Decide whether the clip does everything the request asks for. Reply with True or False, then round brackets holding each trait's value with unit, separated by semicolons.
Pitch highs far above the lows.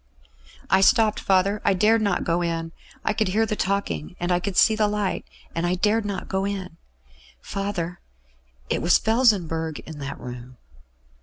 False (3.9 semitones)